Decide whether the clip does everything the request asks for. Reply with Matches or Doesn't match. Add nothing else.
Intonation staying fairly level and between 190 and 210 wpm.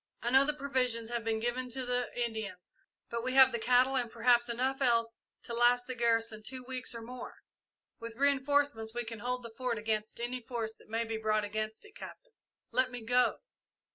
Matches